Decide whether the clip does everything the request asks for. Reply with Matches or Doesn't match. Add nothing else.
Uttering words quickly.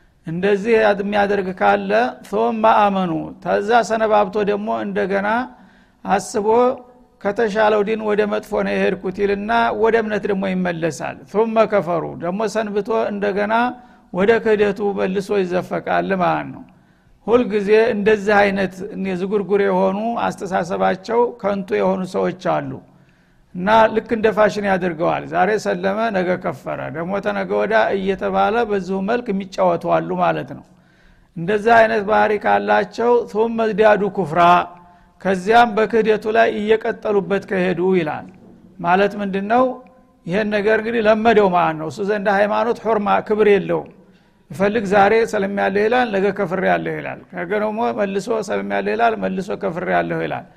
Matches